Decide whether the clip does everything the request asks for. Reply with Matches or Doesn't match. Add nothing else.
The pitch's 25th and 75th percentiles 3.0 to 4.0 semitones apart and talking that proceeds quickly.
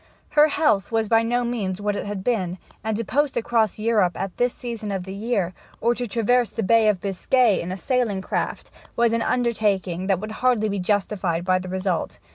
Matches